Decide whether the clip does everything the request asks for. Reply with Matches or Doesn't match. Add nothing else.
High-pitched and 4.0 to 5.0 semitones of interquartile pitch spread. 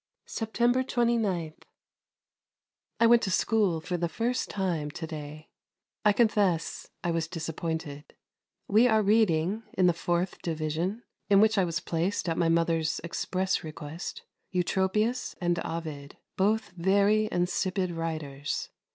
Doesn't match